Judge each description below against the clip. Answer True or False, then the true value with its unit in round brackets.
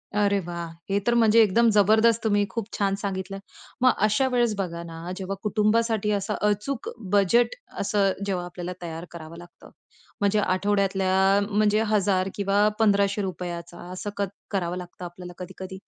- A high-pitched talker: True (200 Hz)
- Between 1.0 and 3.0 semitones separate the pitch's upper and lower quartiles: True (2.5 semitones)